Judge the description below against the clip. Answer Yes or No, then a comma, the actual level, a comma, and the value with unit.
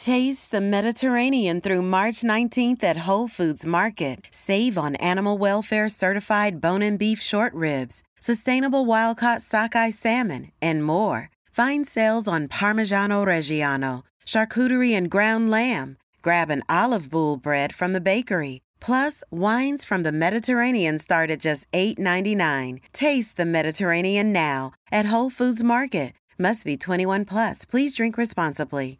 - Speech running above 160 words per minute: No, average, 140 wpm